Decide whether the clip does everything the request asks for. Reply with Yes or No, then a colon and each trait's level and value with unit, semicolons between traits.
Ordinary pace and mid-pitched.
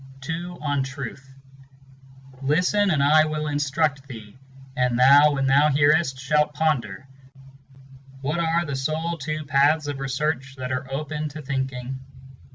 Yes: average, 150 wpm; medium, 145 Hz